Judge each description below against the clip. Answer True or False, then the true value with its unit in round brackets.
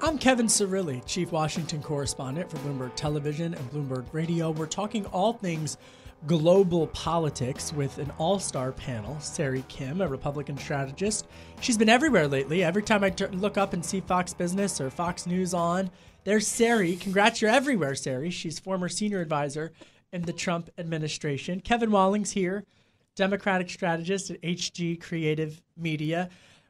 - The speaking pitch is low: False (175 Hz)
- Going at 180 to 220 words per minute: False (155 wpm)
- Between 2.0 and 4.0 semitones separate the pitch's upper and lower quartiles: False (4.4 semitones)